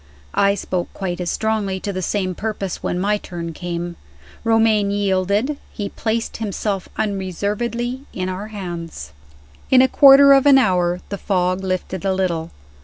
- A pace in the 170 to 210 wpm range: No, average, 155 wpm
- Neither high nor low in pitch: No, high, 195 Hz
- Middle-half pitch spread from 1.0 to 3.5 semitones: Yes, average, 3.2 semitones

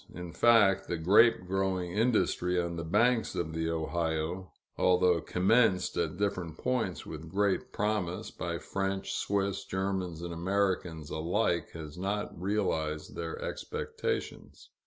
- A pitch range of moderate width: Yes, average, 3.0 semitones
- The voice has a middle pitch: No, very low, 90 Hz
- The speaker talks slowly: Yes, slow, 130 wpm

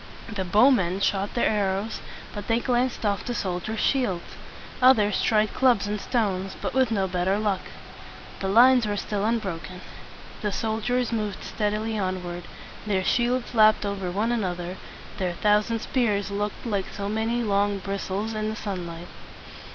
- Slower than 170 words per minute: No, average, 175 wpm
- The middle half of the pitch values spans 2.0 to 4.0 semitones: Yes, average, 2.7 semitones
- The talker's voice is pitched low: No, high, 210 Hz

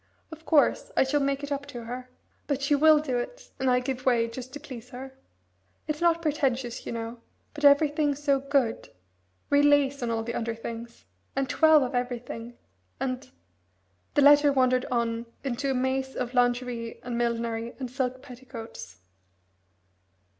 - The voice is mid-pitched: No, very high, 255 Hz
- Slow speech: No, average, 170 wpm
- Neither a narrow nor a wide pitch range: Yes, average, 3.2 semitones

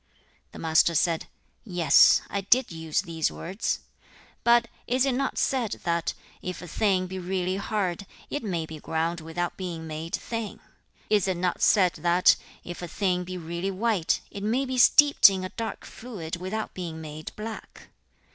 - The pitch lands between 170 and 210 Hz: Yes, medium, 185 Hz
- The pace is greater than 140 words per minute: Yes, average, 175 wpm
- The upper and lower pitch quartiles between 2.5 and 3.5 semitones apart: No, average, 4.0 semitones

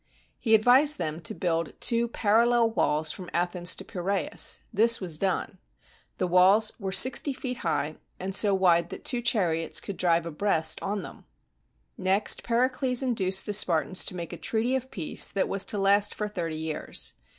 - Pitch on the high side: Yes, high, 195 Hz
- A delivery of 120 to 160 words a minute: No, average, 175 wpm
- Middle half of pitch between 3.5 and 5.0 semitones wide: Yes, average, 4.7 semitones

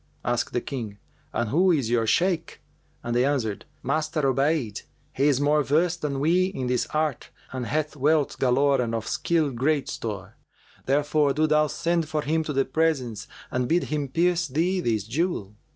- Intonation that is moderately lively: Yes, average, 4.2 semitones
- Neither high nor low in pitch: Yes, medium, 145 Hz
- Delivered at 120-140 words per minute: No, average, 180 wpm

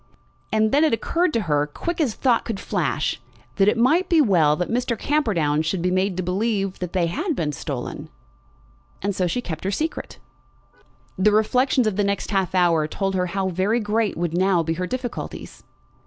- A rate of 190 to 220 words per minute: Yes, average, 195 wpm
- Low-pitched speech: No, high, 195 Hz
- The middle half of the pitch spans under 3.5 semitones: No, average, 4.9 semitones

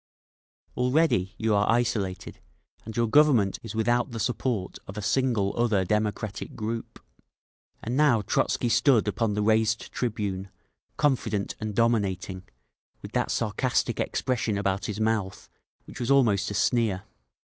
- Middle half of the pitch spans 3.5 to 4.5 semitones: No, average, 3.0 semitones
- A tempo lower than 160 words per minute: Yes, slow, 135 wpm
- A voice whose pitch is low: Yes, low, 110 Hz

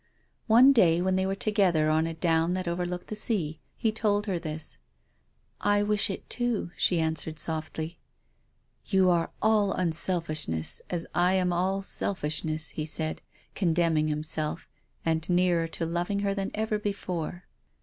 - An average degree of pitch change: Yes, average, 3.6 semitones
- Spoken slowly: No, average, 160 wpm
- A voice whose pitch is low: No, medium, 175 Hz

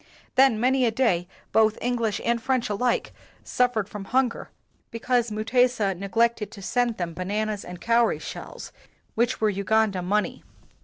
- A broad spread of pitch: No, average, 3.1 semitones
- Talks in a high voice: Yes, high, 225 Hz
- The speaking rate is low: No, average, 155 wpm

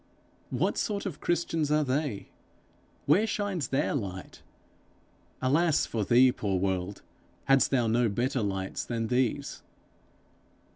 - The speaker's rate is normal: No, slow, 125 wpm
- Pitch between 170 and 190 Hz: No, low, 130 Hz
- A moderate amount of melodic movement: No, wide, 6.3 semitones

